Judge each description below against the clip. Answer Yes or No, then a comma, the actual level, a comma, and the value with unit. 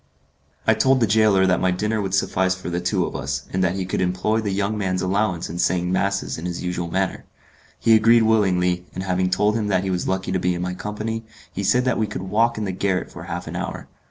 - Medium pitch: No, very low, 95 Hz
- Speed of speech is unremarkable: No, fast, 250 wpm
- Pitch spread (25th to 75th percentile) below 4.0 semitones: Yes, average, 2.8 semitones